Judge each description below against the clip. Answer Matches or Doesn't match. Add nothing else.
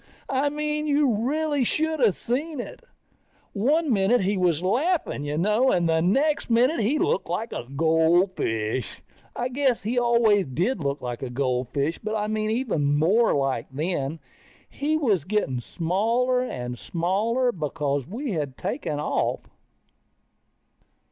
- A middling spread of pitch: Doesn't match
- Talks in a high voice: Matches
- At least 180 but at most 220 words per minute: Doesn't match